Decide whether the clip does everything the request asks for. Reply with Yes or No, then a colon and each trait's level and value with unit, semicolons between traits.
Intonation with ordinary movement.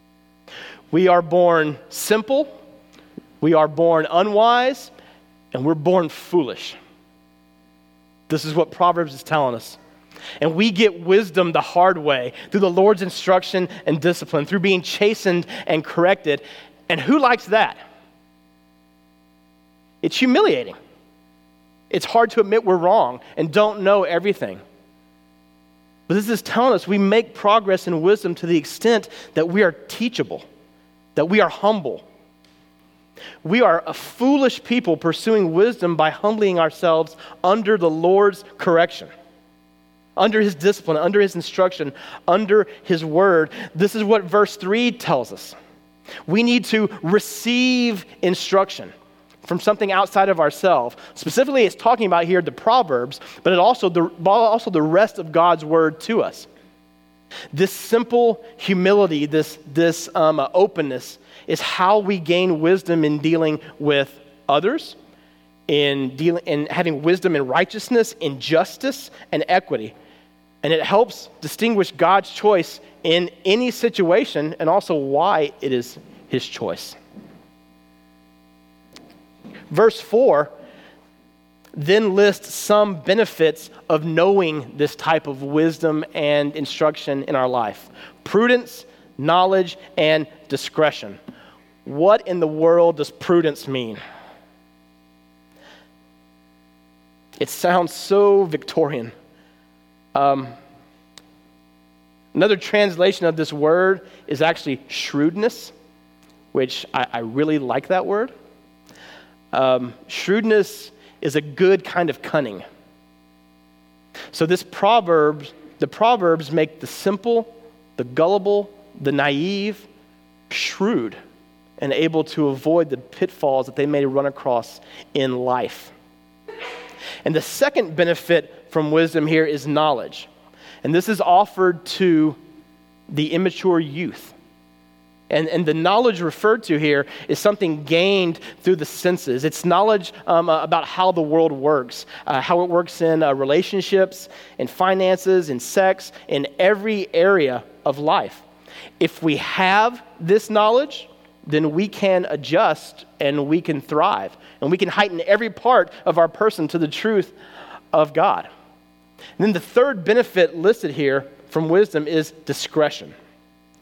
No: wide, 7.3 semitones